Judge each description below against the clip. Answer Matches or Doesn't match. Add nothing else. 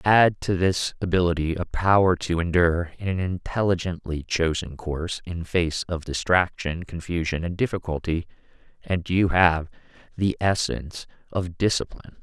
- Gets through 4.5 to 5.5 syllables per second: Matches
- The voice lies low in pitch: Matches